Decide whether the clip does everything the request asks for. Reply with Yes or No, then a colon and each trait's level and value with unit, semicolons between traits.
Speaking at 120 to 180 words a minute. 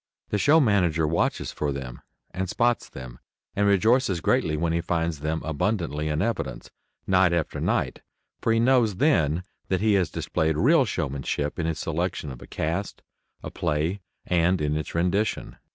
Yes: average, 170 wpm